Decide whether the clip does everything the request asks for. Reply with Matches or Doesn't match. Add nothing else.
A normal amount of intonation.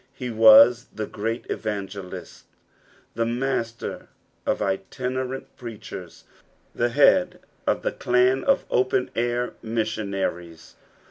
Matches